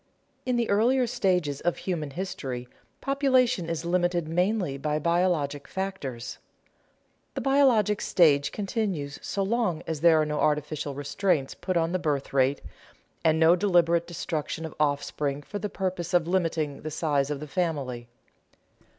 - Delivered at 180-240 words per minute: No, average, 150 wpm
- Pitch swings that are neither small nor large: Yes, average, 4.5 semitones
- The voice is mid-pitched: Yes, medium, 165 Hz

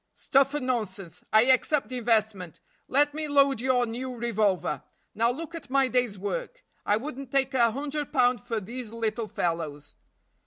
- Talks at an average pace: Yes, average, 165 wpm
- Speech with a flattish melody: No, average, 4.2 semitones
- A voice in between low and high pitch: No, high, 245 Hz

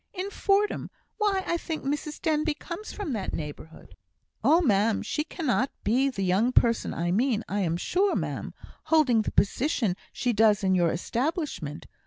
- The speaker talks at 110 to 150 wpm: No, average, 165 wpm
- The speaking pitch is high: Yes, very high, 250 Hz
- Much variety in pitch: Yes, wide, 8.3 semitones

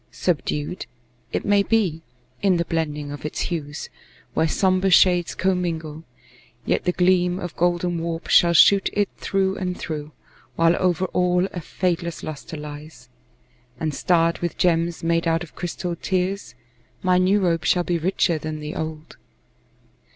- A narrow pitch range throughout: Yes, narrow, 2.3 semitones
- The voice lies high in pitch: No, medium, 170 Hz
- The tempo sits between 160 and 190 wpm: No, average, 150 wpm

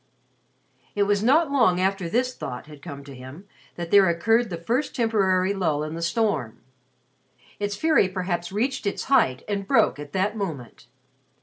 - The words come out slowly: No, average, 170 wpm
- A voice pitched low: No, high, 190 Hz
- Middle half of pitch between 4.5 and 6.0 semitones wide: Yes, average, 5.0 semitones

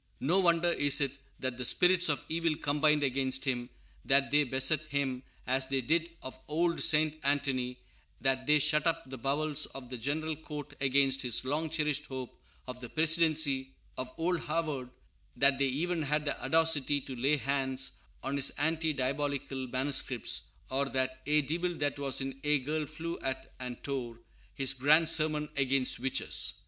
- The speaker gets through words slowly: No, average, 170 wpm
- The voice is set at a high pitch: No, medium, 140 Hz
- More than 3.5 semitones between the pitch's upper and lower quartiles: No, average, 2.8 semitones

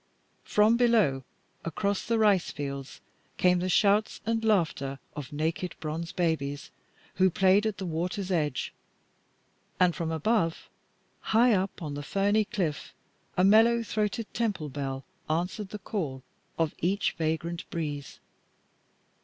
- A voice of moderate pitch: Yes, medium, 180 Hz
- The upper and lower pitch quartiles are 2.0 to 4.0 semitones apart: No, average, 5.1 semitones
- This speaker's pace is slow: Yes, slow, 130 wpm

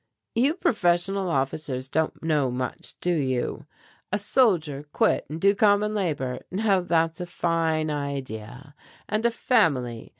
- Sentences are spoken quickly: No, slow, 135 wpm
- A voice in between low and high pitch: Yes, medium, 165 Hz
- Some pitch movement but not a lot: No, wide, 6.2 semitones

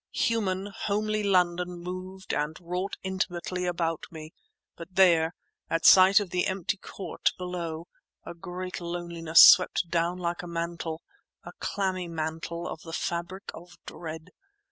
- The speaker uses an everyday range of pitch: No, narrow, 1.8 semitones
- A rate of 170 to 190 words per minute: No, slow, 135 wpm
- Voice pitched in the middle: Yes, medium, 175 Hz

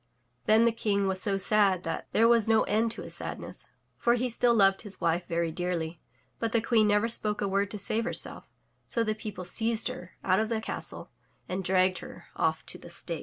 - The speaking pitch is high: Yes, high, 210 Hz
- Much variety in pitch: No, average, 3.4 semitones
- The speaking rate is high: Yes, fast, 220 wpm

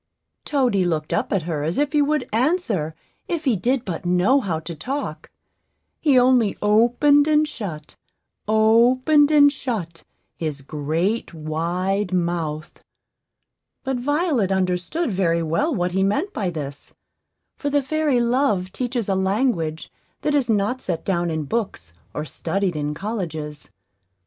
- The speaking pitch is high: Yes, high, 200 Hz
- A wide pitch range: Yes, wide, 7.7 semitones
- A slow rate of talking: No, average, 145 wpm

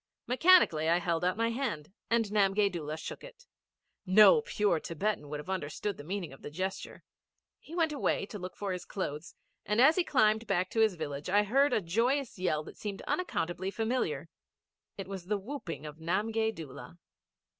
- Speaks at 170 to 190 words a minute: Yes, average, 185 wpm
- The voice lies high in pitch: Yes, high, 195 Hz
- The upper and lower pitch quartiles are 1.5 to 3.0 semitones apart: No, average, 5.1 semitones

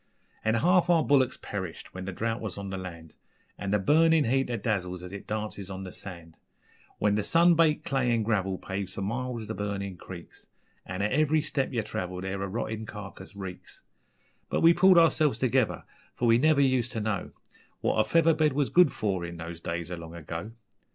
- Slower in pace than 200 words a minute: No, fast, 205 wpm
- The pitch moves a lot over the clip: Yes, wide, 6.1 semitones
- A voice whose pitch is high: No, low, 105 Hz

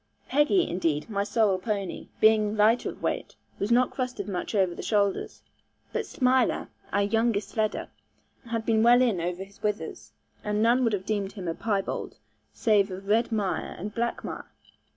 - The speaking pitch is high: Yes, high, 210 Hz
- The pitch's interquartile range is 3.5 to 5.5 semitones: No, average, 2.8 semitones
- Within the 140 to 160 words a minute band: No, average, 170 wpm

